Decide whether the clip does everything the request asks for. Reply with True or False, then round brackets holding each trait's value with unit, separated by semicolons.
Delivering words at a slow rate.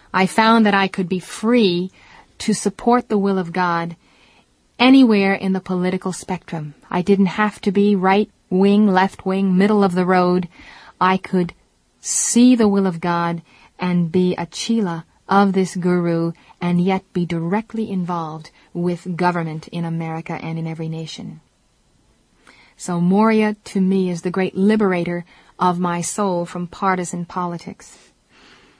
False (150 wpm)